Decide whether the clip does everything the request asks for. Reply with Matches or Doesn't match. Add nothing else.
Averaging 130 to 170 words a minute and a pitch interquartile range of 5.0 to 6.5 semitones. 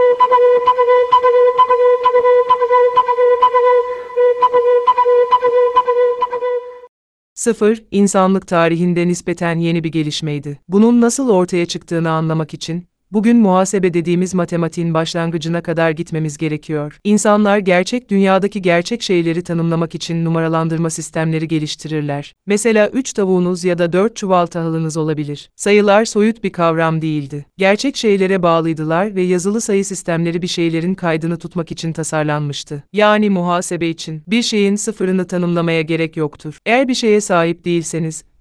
Doesn't match